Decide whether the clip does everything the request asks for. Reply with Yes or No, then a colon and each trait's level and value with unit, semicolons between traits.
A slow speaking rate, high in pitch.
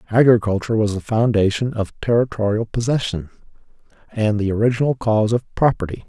No: slow, 130 wpm; low, 110 Hz